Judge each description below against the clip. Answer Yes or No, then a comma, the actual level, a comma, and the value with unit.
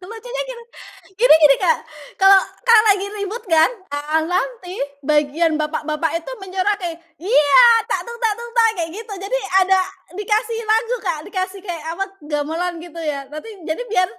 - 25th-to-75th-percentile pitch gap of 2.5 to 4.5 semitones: No, wide, 5.5 semitones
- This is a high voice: Yes, very high, 370 Hz